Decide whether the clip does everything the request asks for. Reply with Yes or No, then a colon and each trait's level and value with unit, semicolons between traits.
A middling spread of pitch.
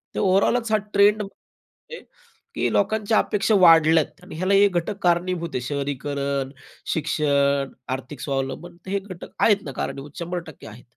No: wide, 5.9 semitones